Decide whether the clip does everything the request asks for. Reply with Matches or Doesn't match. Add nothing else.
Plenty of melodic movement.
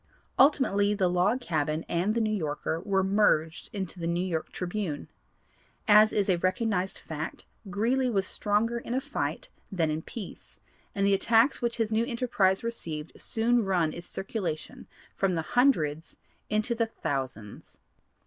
Doesn't match